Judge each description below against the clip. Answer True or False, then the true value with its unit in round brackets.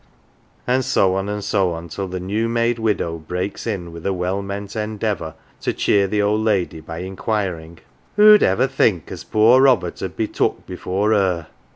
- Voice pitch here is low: True (100 Hz)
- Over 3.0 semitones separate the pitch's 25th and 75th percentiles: True (3.4 semitones)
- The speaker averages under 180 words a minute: False (190 wpm)